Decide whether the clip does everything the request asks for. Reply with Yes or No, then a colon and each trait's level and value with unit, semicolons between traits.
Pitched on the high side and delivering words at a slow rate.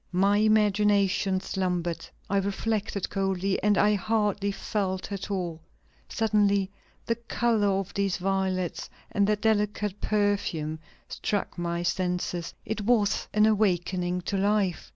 Yes: high, 200 Hz; slow, 125 wpm